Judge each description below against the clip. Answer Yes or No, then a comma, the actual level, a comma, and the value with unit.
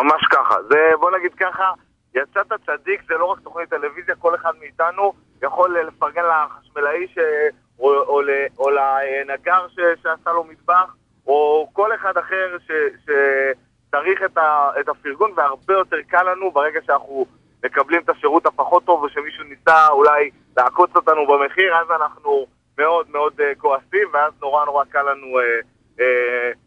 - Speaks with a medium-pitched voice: Yes, medium, 160 Hz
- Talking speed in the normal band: Yes, average, 140 wpm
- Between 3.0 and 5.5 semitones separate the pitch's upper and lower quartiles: Yes, average, 4.7 semitones